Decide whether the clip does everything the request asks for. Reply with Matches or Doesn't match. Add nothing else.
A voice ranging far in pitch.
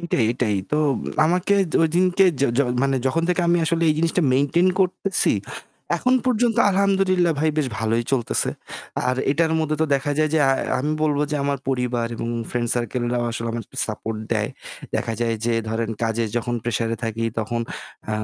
Matches